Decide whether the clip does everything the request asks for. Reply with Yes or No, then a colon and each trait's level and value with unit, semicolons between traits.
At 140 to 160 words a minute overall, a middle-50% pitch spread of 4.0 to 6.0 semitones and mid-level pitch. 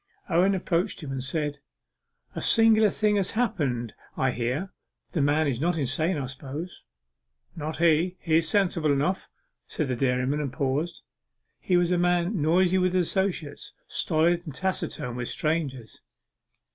Yes: average, 150 wpm; average, 4.7 semitones; medium, 160 Hz